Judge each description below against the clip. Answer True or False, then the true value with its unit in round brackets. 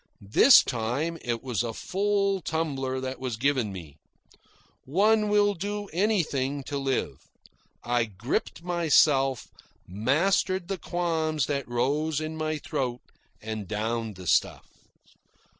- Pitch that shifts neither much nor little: False (6.2 semitones)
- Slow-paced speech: True (125 wpm)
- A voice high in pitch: False (140 Hz)